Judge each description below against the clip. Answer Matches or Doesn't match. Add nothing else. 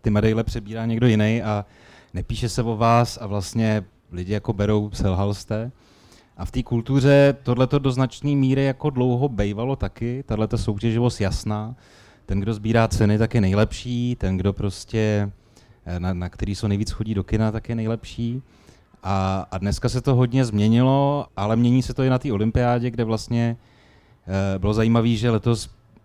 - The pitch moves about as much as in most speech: Matches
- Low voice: Matches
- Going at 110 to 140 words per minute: Doesn't match